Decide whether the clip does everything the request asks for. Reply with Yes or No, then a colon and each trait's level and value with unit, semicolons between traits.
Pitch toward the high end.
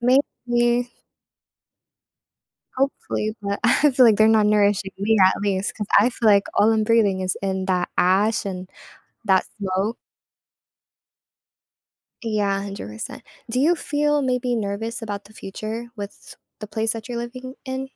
Yes: high, 215 Hz